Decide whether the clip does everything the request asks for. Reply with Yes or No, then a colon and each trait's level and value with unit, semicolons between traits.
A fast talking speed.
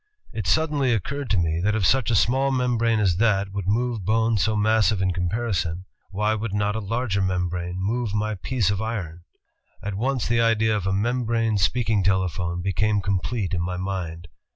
No: average, 190 wpm